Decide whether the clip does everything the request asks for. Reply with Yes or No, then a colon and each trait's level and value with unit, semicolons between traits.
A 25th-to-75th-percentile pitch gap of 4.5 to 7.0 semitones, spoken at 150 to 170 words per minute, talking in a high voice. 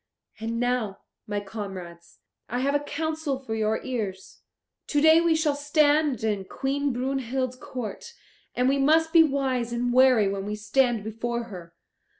Yes: average, 4.8 semitones; average, 155 wpm; very high, 250 Hz